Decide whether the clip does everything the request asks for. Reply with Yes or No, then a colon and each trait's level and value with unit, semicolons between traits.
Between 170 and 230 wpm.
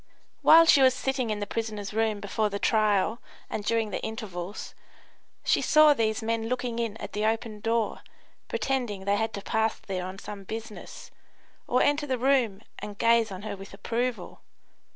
Yes: average, 175 wpm